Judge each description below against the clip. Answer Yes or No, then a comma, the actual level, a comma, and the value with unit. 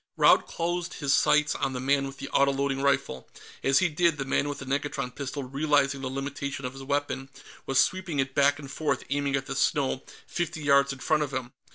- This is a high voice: No, medium, 140 Hz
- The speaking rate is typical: No, fast, 215 wpm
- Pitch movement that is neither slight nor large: No, narrow, 1.3 semitones